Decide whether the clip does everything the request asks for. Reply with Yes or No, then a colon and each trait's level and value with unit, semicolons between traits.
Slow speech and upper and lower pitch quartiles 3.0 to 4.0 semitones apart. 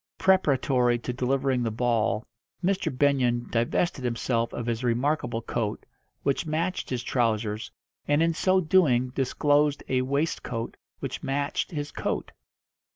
Yes: slow, 130 wpm; average, 3.6 semitones